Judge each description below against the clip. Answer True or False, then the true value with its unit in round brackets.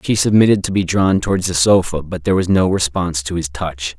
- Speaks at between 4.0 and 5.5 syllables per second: False (6.0 syllables/s)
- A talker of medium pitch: False (90 Hz)